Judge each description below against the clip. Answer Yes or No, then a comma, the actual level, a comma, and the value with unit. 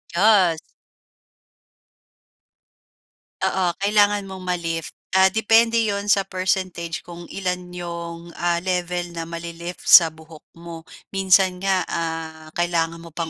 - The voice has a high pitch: No, medium, 175 Hz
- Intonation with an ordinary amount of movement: No, narrow, 2.2 semitones